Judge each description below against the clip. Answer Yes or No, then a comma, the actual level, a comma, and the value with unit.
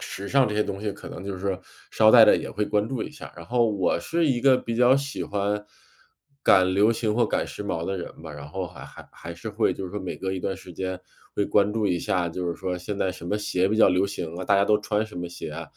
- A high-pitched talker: No, low, 100 Hz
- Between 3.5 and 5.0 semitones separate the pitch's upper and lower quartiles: No, average, 2.9 semitones